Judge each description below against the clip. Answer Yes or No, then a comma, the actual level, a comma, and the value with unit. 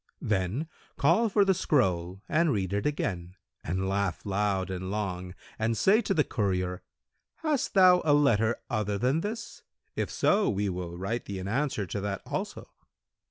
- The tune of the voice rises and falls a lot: Yes, wide, 8.0 semitones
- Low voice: Yes, low, 105 Hz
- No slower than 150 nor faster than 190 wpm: Yes, average, 165 wpm